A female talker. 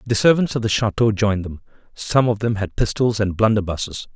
No: male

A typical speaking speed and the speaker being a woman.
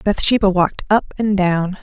Yes: average, 165 wpm; female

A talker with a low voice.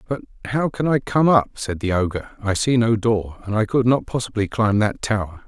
Yes: low, 110 Hz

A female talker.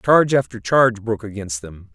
No: male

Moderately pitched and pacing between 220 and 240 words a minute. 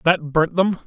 No: medium, 170 Hz; fast, 210 wpm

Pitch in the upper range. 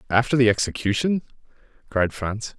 No: low, 115 Hz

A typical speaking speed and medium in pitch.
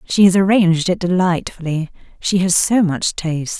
Yes: average, 165 wpm; medium, 180 Hz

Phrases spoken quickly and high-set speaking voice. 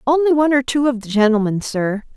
Yes: fast, 220 wpm; very high, 250 Hz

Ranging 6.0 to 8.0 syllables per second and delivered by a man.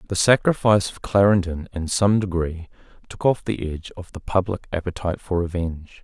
No: 5.6 syllables/s; male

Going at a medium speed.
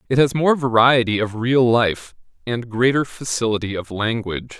Yes: average, 155 wpm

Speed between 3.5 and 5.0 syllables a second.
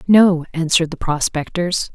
Yes: 4.6 syllables/s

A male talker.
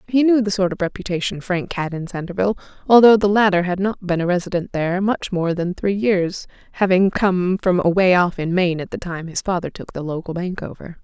No: female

